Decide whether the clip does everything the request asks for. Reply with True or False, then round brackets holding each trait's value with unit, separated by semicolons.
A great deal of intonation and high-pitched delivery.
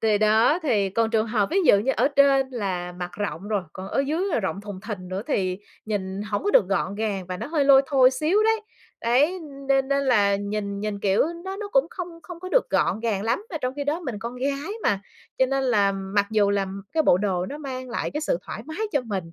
True (5.8 semitones; 225 Hz)